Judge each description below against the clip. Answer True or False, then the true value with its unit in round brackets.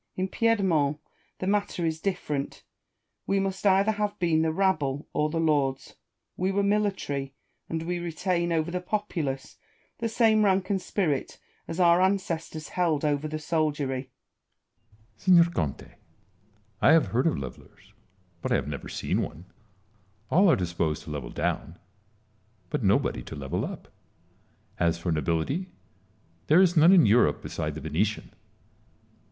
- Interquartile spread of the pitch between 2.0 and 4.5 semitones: False (5.6 semitones)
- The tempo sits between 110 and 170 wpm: True (150 wpm)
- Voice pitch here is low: False (165 Hz)